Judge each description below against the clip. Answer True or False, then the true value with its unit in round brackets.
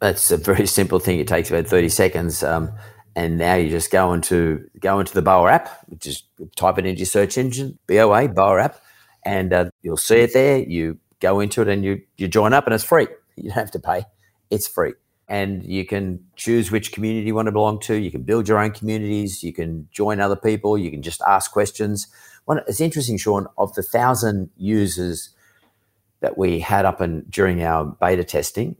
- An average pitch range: True (3.2 semitones)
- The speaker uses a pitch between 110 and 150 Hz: False (100 Hz)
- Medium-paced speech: False (210 wpm)